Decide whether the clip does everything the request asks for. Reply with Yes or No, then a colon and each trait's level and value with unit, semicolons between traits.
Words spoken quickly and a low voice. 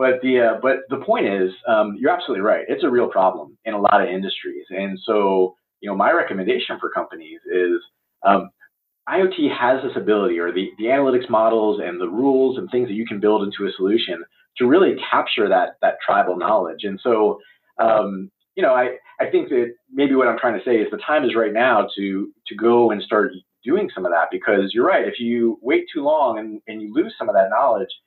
Yes: fast, 220 wpm; low, 125 Hz